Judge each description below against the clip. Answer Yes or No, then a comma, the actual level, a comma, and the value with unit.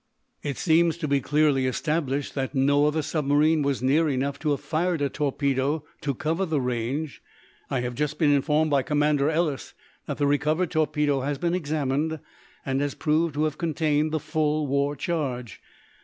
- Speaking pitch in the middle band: Yes, medium, 150 Hz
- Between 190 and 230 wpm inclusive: No, average, 175 wpm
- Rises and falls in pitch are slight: Yes, narrow, 2.1 semitones